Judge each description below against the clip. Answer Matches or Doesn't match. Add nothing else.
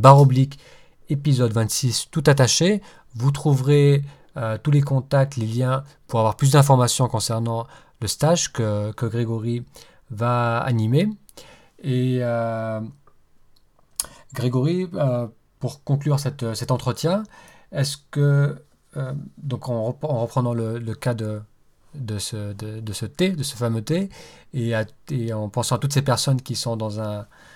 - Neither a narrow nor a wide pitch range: Matches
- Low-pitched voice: Matches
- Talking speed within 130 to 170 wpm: Matches